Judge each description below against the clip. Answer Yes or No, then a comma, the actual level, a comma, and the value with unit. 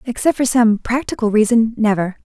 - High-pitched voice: Yes, high, 230 Hz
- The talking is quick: No, slow, 130 wpm